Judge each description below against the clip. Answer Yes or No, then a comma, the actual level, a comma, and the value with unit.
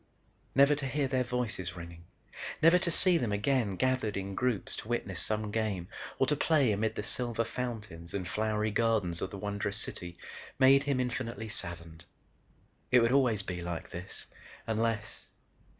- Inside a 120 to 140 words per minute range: No, average, 165 wpm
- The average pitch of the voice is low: Yes, low, 110 Hz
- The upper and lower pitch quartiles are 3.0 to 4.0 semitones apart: No, average, 4.6 semitones